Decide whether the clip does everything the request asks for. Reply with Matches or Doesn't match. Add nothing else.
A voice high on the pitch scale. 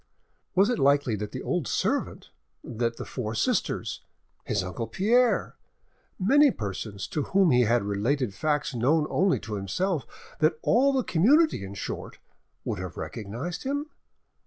Doesn't match